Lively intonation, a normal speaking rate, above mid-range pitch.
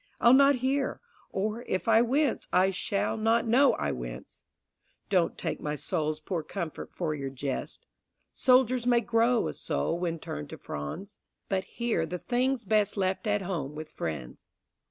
Yes: wide, 7.2 semitones; average, 165 wpm; high, 195 Hz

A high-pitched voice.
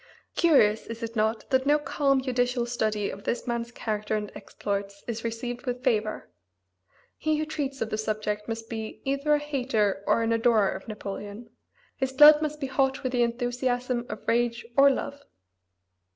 Yes: high, 240 Hz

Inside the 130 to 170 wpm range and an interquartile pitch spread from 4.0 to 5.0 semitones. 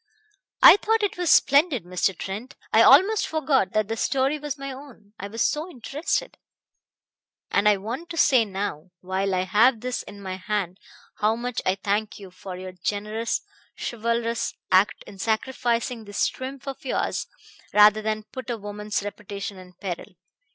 Yes: average, 165 wpm; average, 4.7 semitones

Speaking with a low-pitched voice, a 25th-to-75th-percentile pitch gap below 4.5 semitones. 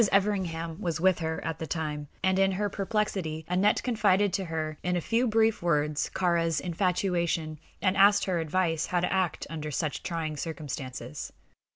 No: medium, 175 Hz; average, 3.3 semitones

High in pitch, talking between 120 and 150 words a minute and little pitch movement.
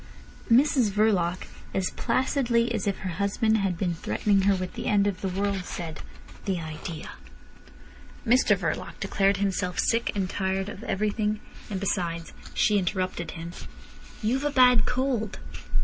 No: high, 200 Hz; average, 145 wpm; average, 3.2 semitones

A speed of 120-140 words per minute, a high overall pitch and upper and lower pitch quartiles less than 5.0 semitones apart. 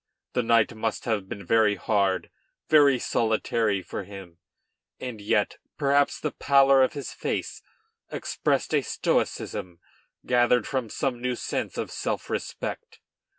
No: slow, 135 wpm; low, 115 Hz; average, 4.2 semitones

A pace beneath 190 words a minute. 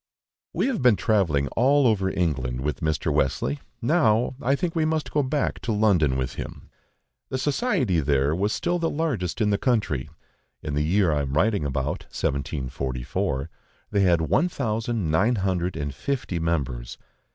Yes: average, 165 wpm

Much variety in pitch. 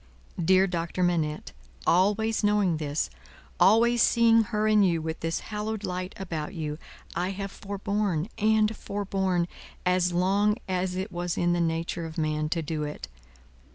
No: average, 3.8 semitones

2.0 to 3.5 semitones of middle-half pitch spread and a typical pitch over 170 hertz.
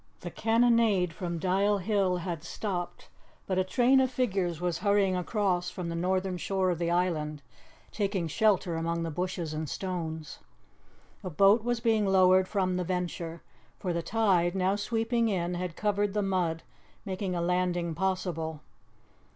Yes: average, 2.8 semitones; medium, 185 Hz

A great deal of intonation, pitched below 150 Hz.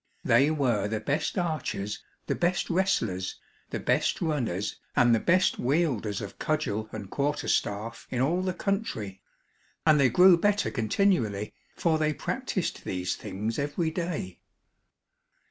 Yes: wide, 8.1 semitones; medium, 140 Hz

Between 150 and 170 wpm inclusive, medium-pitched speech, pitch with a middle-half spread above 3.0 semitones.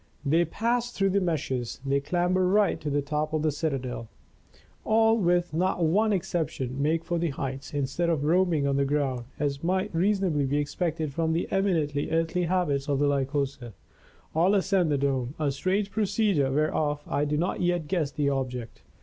No: average, 180 wpm; medium, 155 Hz; average, 4.4 semitones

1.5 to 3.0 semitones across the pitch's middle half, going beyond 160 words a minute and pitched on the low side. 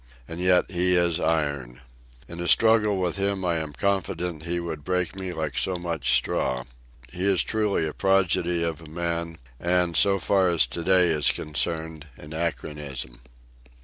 Yes: narrow, 2.5 semitones; average, 175 wpm; very low, 85 Hz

